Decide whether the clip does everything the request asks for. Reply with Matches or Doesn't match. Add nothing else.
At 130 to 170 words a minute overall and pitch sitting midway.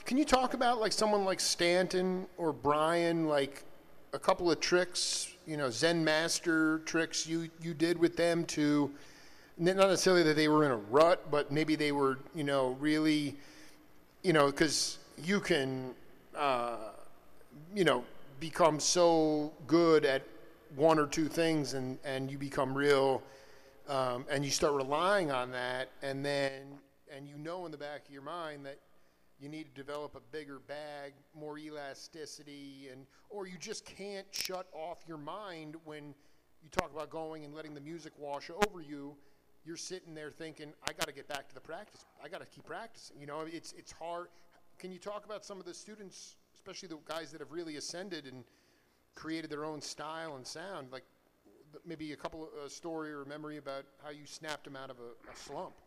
Doesn't match